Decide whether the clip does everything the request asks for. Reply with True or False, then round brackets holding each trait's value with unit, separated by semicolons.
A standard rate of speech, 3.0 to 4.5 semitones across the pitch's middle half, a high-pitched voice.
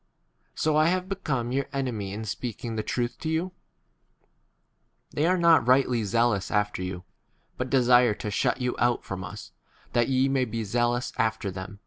False (180 wpm; 4.1 semitones; 120 Hz)